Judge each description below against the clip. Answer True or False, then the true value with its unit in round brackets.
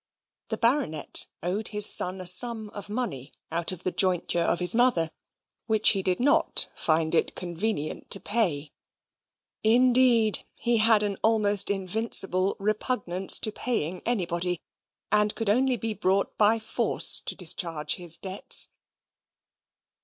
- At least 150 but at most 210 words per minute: False (140 wpm)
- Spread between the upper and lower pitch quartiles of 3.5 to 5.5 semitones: True (4.0 semitones)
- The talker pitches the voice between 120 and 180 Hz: False (200 Hz)